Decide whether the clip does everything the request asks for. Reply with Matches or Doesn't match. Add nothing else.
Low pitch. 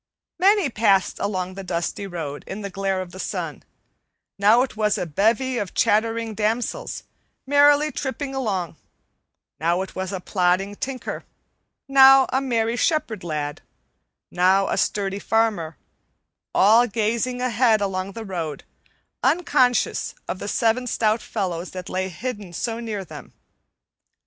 Doesn't match